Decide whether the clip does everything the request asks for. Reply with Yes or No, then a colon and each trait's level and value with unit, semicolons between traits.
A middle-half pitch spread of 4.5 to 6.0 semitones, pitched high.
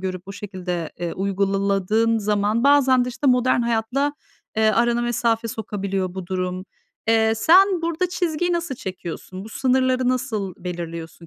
Yes: average, 5.2 semitones; high, 220 Hz